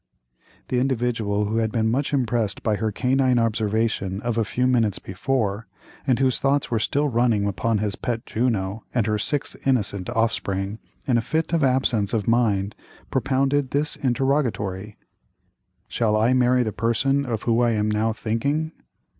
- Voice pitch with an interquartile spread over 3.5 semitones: No, average, 3.2 semitones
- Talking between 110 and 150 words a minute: No, average, 165 wpm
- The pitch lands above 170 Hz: No, low, 115 Hz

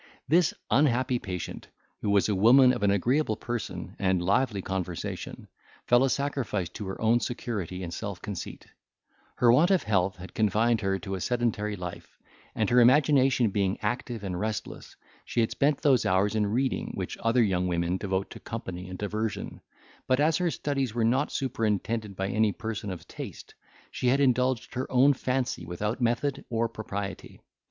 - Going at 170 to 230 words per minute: Yes, average, 175 wpm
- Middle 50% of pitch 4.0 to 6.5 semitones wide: Yes, average, 4.6 semitones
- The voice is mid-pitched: No, low, 110 Hz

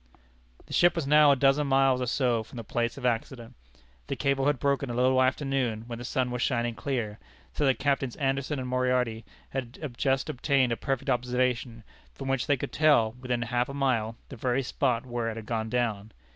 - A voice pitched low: Yes, low, 125 Hz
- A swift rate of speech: Yes, fast, 210 wpm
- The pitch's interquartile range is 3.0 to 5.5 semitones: No, narrow, 2.4 semitones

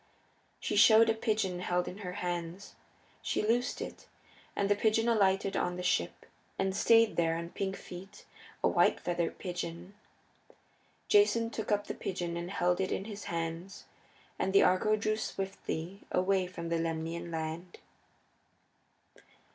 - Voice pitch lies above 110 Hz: Yes, high, 190 Hz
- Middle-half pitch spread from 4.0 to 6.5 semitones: No, average, 3.2 semitones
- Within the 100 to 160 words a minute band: Yes, average, 150 wpm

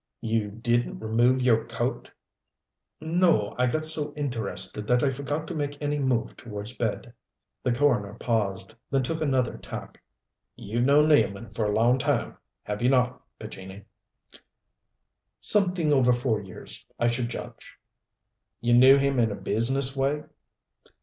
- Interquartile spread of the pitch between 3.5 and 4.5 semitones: Yes, average, 4.1 semitones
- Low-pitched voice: Yes, low, 125 Hz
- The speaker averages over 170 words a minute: No, average, 145 wpm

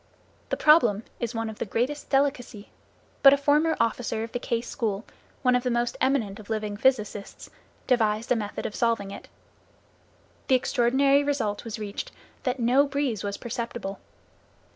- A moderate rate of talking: Yes, average, 165 wpm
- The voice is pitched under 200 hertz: No, high, 235 Hz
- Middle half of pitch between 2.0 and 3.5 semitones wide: No, average, 4.1 semitones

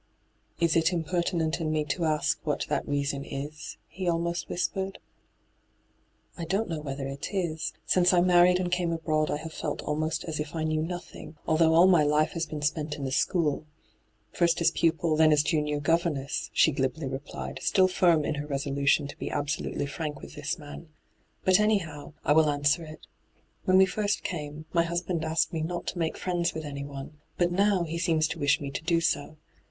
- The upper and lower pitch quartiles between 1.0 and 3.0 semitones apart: Yes, average, 2.7 semitones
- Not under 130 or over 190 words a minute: No, fast, 205 wpm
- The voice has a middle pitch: Yes, medium, 160 Hz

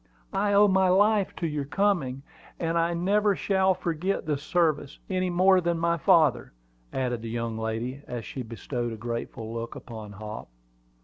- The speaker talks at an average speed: Yes, average, 170 wpm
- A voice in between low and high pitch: Yes, medium, 155 Hz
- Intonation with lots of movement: Yes, wide, 7.8 semitones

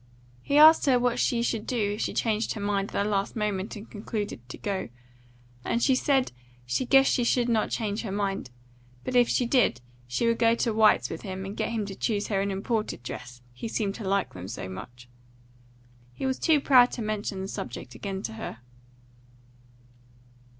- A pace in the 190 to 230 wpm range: Yes, average, 200 wpm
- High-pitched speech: Yes, high, 210 Hz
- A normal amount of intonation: Yes, average, 3.5 semitones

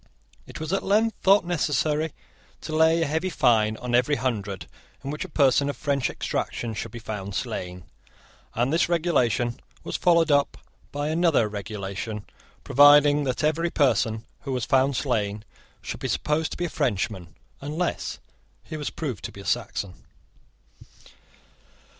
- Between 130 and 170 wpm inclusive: Yes, average, 155 wpm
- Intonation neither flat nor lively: No, wide, 6.1 semitones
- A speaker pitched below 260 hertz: Yes, medium, 140 Hz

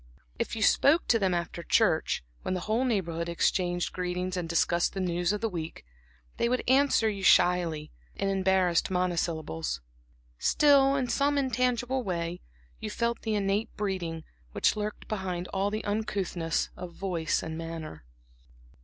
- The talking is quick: No, average, 155 wpm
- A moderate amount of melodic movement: Yes, average, 4.3 semitones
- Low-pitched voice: No, medium, 185 Hz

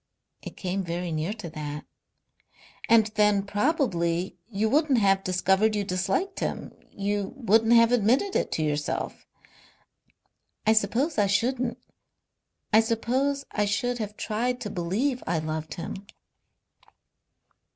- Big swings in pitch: No, average, 4.3 semitones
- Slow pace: Yes, slow, 130 wpm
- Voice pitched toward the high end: Yes, high, 210 Hz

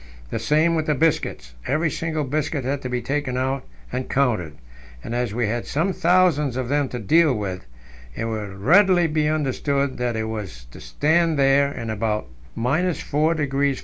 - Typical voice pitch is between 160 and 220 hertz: No, low, 135 Hz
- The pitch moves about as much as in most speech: Yes, average, 4.8 semitones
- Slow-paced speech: No, average, 180 wpm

